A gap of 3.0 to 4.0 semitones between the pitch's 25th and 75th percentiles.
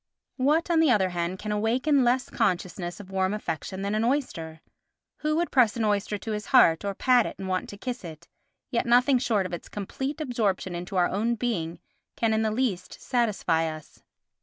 No: average, 5.1 semitones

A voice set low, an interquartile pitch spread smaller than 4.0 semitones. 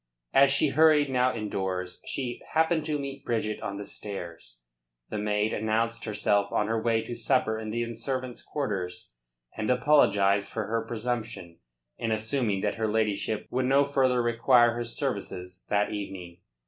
Yes: low, 110 Hz; average, 3.6 semitones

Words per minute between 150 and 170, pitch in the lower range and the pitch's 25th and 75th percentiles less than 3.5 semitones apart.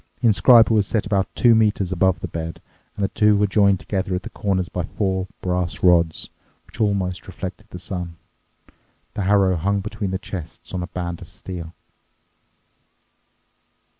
Yes: average, 165 wpm; very low, 95 Hz; narrow, 2.4 semitones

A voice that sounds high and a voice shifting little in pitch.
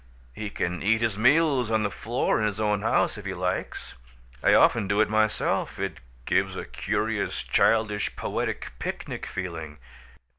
No: low, 105 Hz; narrow, 2.3 semitones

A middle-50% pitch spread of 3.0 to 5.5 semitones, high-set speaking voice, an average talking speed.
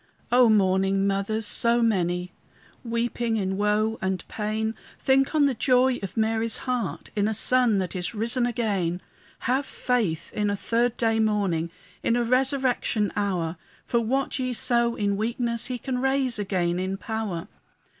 Yes: average, 3.8 semitones; high, 220 Hz; average, 155 wpm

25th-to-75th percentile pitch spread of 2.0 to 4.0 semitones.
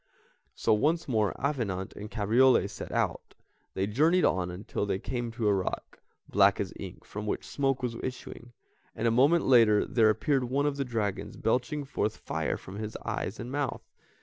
No: average, 4.5 semitones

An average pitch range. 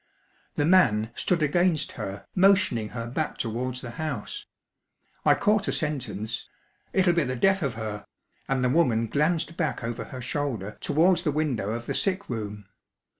No: wide, 6.6 semitones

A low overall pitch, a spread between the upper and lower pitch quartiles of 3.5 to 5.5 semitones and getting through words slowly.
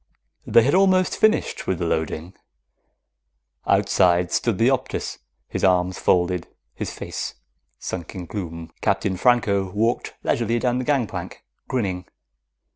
Yes: low, 100 Hz; average, 5.2 semitones; slow, 130 wpm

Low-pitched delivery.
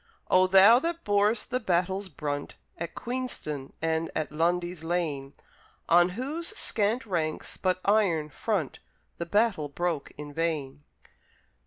No: medium, 175 Hz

